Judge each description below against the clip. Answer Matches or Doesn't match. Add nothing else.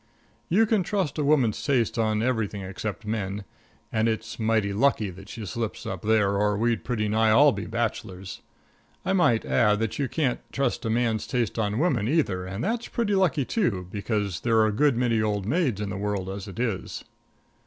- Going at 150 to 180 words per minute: Doesn't match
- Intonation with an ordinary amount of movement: Matches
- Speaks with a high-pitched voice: Doesn't match